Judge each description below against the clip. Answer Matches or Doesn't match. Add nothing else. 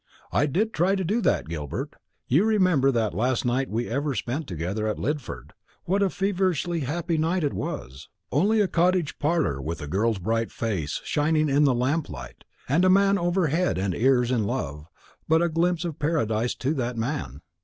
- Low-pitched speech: Doesn't match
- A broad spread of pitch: Matches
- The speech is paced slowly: Doesn't match